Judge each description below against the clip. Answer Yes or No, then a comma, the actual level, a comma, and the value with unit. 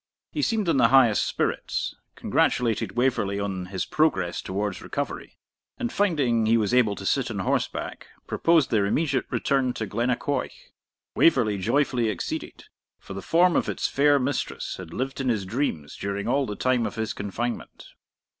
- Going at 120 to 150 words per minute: No, average, 165 wpm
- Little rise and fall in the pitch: No, average, 5.3 semitones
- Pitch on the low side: Yes, low, 120 Hz